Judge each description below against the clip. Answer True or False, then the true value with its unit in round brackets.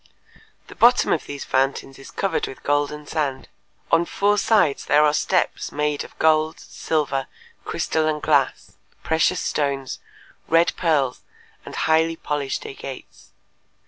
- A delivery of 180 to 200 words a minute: False (135 wpm)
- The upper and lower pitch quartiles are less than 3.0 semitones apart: True (2.6 semitones)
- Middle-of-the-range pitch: True (150 Hz)